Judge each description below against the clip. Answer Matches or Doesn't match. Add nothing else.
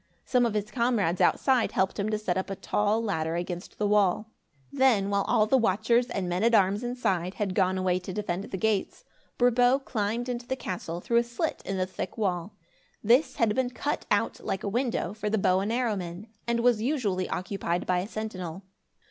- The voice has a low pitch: Doesn't match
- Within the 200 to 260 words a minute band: Matches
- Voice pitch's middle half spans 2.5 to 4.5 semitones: Matches